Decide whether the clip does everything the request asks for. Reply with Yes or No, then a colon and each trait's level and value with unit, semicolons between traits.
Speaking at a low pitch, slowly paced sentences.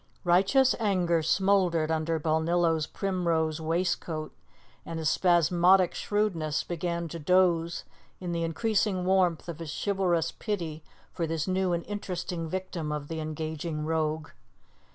No: medium, 170 Hz; slow, 130 wpm